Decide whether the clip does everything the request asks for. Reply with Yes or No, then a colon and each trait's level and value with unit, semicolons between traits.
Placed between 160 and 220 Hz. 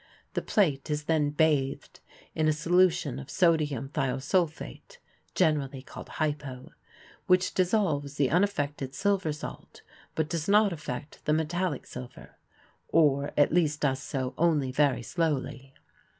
No: medium, 150 Hz